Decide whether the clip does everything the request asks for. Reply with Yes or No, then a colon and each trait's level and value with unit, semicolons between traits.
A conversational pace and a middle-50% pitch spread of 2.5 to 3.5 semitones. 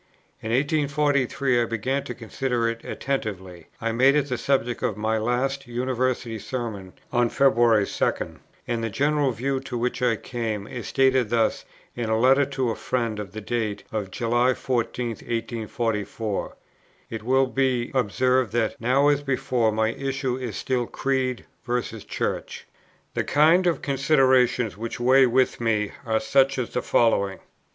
Yes: average, 160 wpm; average, 2.9 semitones